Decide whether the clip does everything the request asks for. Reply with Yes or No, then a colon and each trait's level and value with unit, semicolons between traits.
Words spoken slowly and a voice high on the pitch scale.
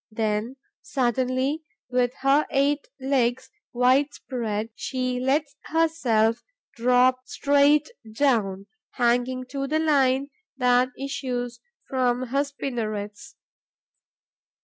Yes: slow, 95 wpm; very high, 255 Hz